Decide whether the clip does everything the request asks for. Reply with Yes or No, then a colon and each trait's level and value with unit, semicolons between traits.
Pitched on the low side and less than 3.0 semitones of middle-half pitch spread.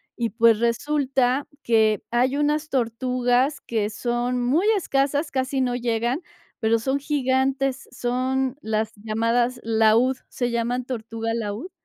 No: high, 245 Hz; narrow, 2.6 semitones